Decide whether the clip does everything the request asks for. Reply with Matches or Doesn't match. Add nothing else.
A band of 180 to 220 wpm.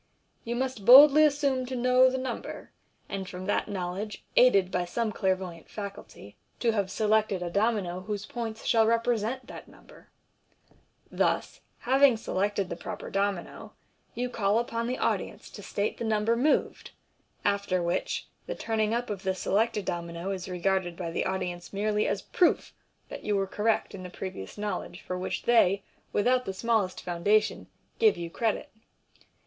Doesn't match